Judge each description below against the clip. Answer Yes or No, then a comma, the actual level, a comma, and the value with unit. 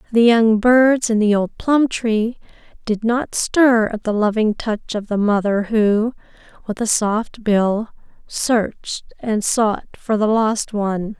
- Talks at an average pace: Yes, average, 160 wpm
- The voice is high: Yes, high, 220 Hz